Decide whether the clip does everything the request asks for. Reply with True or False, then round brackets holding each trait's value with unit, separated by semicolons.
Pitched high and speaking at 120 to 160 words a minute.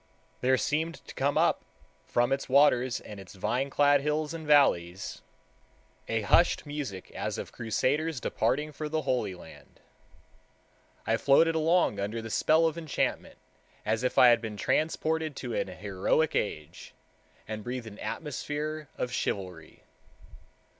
False (130 Hz; 145 wpm)